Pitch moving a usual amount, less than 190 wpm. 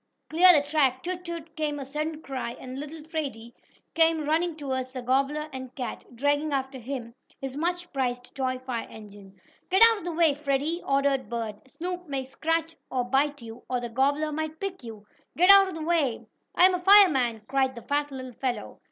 No: average, 4.0 semitones; average, 195 wpm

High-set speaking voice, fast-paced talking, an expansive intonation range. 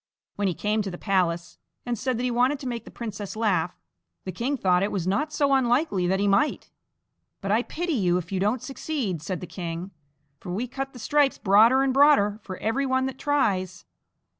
Yes: high, 215 Hz; fast, 215 wpm; wide, 5.9 semitones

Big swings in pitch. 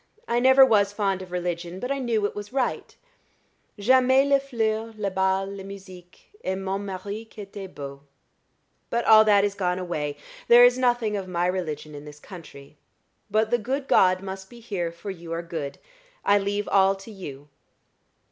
No: average, 3.7 semitones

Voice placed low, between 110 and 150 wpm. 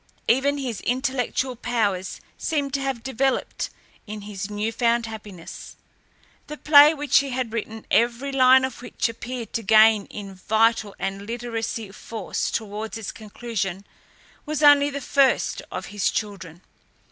No: high, 230 Hz; average, 145 wpm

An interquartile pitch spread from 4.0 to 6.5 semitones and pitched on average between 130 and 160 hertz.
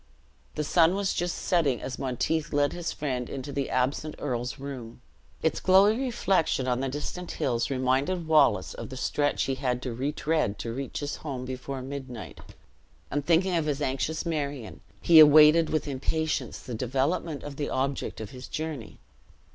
No: average, 3.5 semitones; medium, 140 Hz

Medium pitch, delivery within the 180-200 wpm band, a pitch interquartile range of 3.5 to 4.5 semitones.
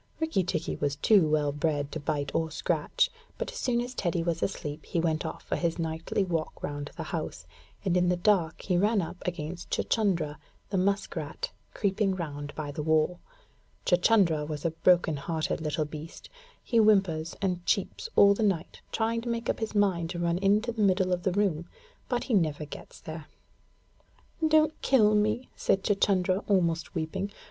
Yes: medium, 175 Hz; average, 185 wpm; average, 4.2 semitones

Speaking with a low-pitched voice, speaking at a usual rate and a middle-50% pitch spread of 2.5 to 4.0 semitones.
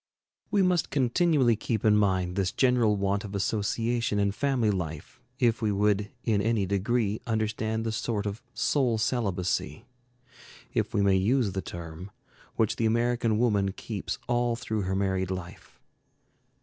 Yes: low, 110 Hz; average, 150 wpm; average, 3.1 semitones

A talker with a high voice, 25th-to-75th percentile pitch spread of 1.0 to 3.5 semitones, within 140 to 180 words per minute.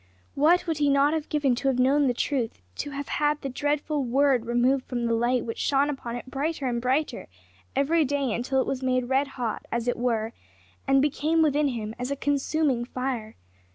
No: very high, 270 Hz; average, 2.9 semitones; fast, 205 wpm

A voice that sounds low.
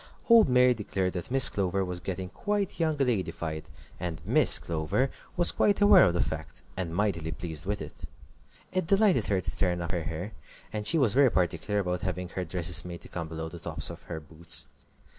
Yes: very low, 90 Hz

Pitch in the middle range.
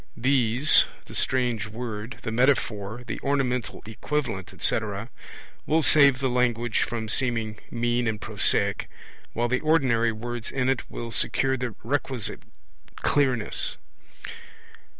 No: low, 120 Hz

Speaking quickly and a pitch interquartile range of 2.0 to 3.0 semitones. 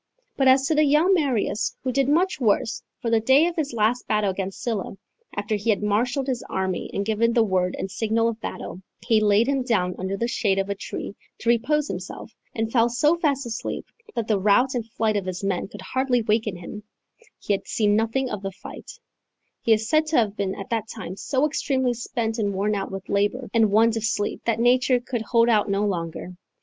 No: fast, 220 wpm; average, 3.8 semitones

